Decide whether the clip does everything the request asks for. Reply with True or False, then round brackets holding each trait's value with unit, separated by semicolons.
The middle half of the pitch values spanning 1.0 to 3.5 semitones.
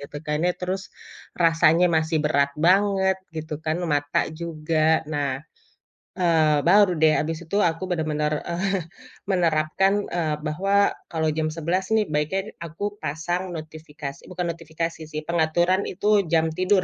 True (2.8 semitones)